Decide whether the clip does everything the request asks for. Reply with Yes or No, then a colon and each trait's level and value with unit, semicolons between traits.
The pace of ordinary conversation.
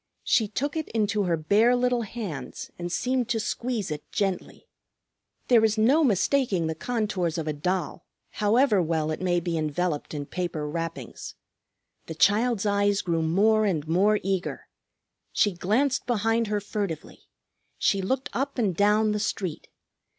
Yes: average, 155 wpm